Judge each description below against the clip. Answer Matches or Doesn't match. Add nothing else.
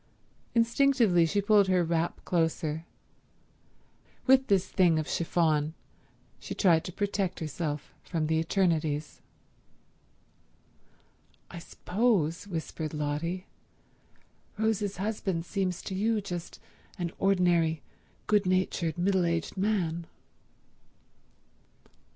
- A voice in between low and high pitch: Matches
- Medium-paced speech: Doesn't match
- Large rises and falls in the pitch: Doesn't match